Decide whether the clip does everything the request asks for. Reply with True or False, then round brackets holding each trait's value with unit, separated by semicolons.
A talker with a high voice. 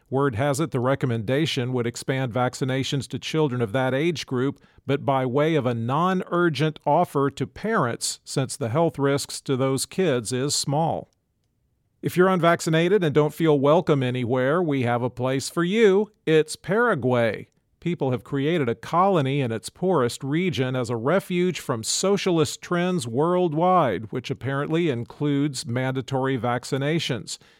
False (140 Hz)